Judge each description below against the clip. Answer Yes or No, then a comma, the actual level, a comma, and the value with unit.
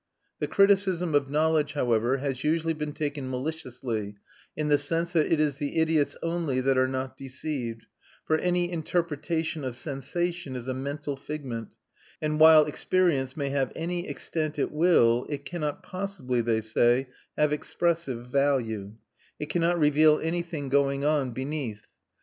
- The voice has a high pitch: No, medium, 145 Hz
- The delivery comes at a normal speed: Yes, average, 150 wpm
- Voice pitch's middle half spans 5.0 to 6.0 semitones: No, average, 3.7 semitones